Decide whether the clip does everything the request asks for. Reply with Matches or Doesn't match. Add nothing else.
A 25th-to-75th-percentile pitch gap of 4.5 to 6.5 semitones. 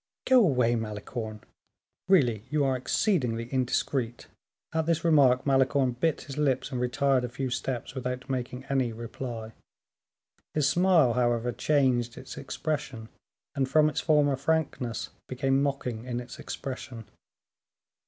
Doesn't match